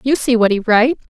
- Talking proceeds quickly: Yes, fast, 265 wpm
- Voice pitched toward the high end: Yes, high, 240 Hz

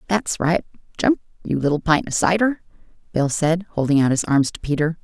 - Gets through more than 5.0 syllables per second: Yes, 5.5 syllables/s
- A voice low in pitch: No, medium, 165 Hz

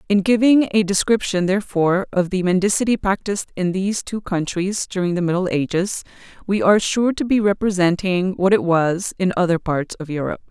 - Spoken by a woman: Yes, female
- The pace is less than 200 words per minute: Yes, average, 175 wpm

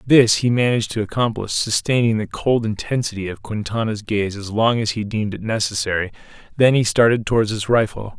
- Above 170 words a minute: Yes, average, 185 wpm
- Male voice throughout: Yes, male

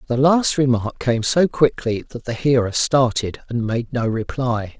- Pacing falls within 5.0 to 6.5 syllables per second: No, 4.3 syllables/s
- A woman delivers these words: No, male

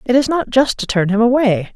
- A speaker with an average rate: No, fast, 275 wpm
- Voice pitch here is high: Yes, high, 235 Hz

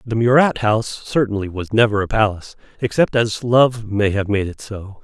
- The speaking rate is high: No, average, 190 wpm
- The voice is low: Yes, low, 110 Hz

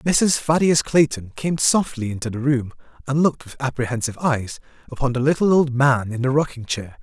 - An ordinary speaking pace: Yes, average, 190 wpm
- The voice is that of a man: Yes, male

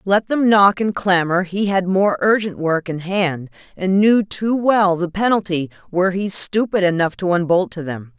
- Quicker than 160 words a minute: Yes, average, 190 wpm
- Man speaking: No, female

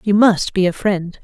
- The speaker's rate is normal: No, fast, 245 wpm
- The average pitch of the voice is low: No, high, 195 Hz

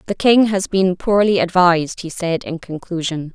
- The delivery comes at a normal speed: Yes, average, 180 wpm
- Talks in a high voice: No, medium, 180 Hz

